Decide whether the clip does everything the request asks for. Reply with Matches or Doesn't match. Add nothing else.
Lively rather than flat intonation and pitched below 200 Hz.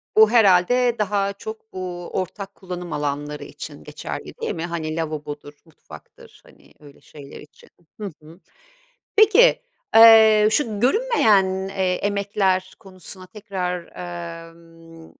Doesn't match